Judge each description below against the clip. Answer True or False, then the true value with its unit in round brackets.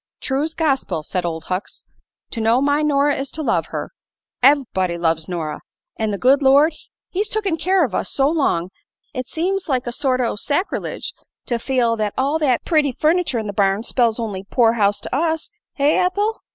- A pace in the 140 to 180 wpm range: False (190 wpm)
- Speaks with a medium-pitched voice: False (265 Hz)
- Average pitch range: False (6.1 semitones)